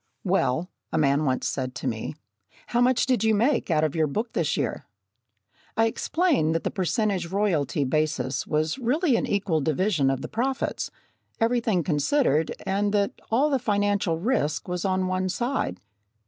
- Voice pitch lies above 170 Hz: Yes, medium, 185 Hz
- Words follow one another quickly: No, average, 165 wpm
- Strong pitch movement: Yes, wide, 6.8 semitones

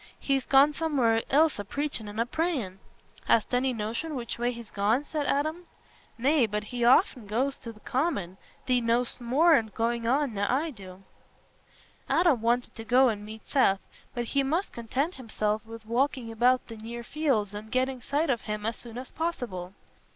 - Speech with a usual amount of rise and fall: Yes, average, 4.0 semitones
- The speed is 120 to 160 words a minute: No, average, 180 wpm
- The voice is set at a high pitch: Yes, high, 240 Hz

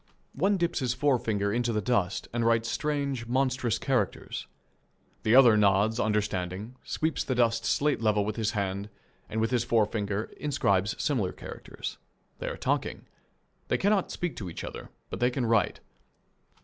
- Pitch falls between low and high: No, low, 115 Hz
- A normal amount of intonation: Yes, average, 3.9 semitones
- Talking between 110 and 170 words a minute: Yes, average, 160 wpm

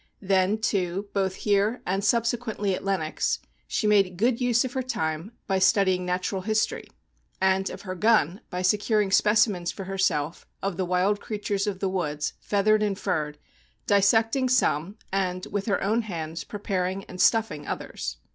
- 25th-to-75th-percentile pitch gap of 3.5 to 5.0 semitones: No, narrow, 2.6 semitones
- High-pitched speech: Yes, high, 195 Hz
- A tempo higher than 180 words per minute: No, average, 165 wpm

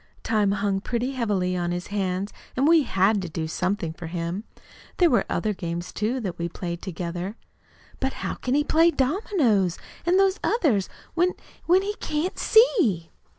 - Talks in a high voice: Yes, high, 205 Hz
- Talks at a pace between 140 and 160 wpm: No, average, 170 wpm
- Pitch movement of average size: No, wide, 8.6 semitones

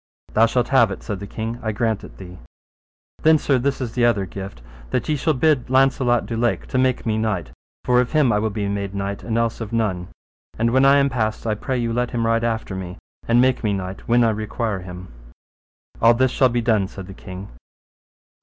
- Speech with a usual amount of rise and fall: Yes, average, 3.6 semitones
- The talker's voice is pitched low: Yes, low, 115 Hz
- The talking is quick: Yes, fast, 230 wpm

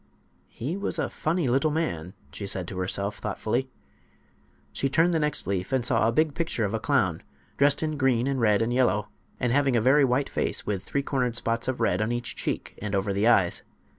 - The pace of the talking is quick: Yes, fast, 215 wpm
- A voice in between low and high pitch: No, low, 120 Hz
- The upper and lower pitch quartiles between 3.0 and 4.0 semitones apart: No, average, 5.0 semitones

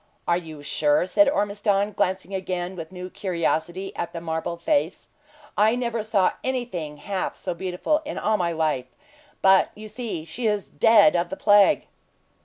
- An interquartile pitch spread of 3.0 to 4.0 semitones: Yes, average, 3.7 semitones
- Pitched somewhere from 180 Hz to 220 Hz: Yes, high, 190 Hz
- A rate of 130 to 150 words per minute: No, average, 165 wpm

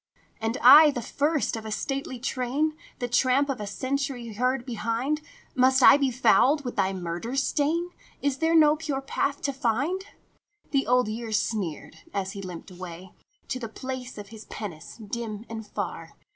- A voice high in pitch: Yes, very high, 250 Hz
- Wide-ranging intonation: No, average, 4.4 semitones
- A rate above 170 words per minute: Yes, average, 180 wpm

